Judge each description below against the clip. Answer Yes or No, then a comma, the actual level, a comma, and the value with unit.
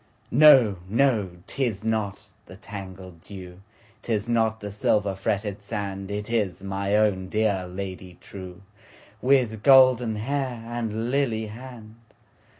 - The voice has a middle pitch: No, low, 105 Hz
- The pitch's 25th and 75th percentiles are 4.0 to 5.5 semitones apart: No, average, 2.8 semitones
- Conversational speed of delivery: No, slow, 110 wpm